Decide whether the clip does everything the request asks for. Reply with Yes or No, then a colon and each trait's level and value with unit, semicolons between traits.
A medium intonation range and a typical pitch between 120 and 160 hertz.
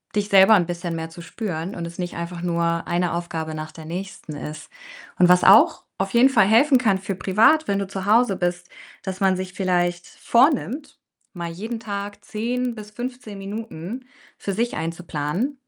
No: average, 4.3 semitones; high, 190 Hz